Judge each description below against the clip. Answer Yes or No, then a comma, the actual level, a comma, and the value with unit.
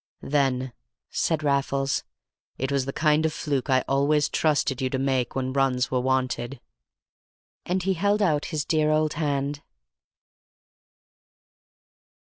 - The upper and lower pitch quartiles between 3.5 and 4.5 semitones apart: No, narrow, 2.5 semitones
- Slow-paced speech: Yes, slow, 130 wpm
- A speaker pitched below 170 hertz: Yes, medium, 140 Hz